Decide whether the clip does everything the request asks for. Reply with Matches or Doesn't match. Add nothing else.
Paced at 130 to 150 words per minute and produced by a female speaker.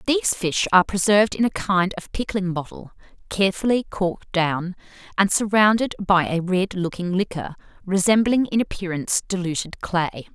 Matches